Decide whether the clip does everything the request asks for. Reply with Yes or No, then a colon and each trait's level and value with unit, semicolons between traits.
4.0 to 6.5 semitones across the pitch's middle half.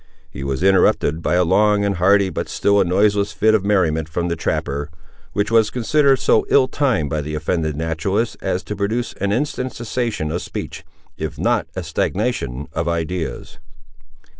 Yes: average, 4.7 semitones